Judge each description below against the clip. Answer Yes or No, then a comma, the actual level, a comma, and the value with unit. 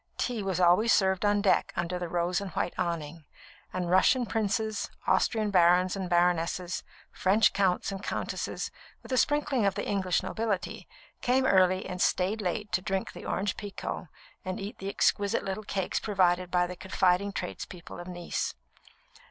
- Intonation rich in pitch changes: No, narrow, 2.4 semitones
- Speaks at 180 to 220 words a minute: No, average, 165 wpm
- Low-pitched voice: No, high, 190 Hz